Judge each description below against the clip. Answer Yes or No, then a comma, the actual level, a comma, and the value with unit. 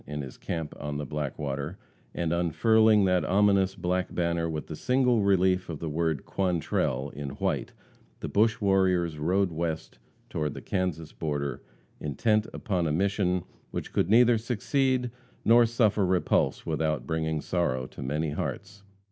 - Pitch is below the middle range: Yes, very low, 90 Hz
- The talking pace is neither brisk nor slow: Yes, average, 150 wpm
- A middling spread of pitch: Yes, average, 4.6 semitones